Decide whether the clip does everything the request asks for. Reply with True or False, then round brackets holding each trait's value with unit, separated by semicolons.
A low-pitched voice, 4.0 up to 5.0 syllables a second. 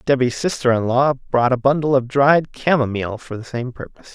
False (130 Hz; 5.4 syllables/s)